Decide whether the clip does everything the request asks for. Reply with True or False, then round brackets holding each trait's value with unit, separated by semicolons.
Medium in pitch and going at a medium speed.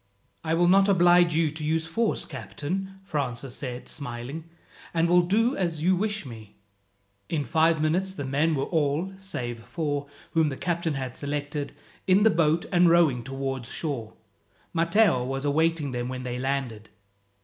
True (155 Hz; 160 wpm)